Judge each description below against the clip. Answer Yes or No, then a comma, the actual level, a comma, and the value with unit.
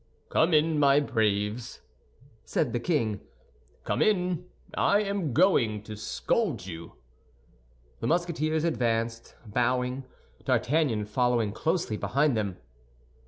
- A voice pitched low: Yes, low, 125 Hz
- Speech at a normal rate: No, slow, 110 wpm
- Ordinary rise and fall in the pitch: No, wide, 6.6 semitones